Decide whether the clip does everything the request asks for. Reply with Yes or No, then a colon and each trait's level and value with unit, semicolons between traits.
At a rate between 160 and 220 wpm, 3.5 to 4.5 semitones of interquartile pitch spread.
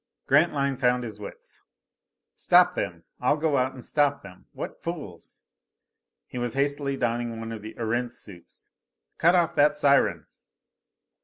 No: average, 145 wpm; average, 4.0 semitones